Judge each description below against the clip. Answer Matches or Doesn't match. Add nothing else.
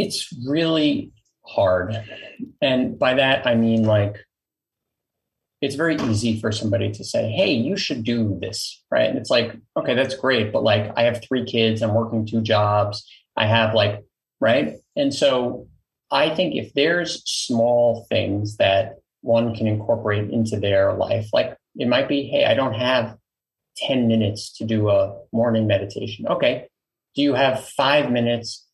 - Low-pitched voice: Matches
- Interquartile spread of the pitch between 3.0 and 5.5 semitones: Matches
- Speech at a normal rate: Matches